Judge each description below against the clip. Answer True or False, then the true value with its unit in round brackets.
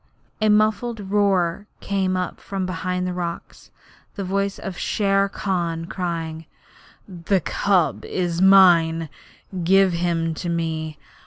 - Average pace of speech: False (125 wpm)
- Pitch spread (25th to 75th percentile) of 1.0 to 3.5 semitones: True (2.7 semitones)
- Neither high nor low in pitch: True (180 Hz)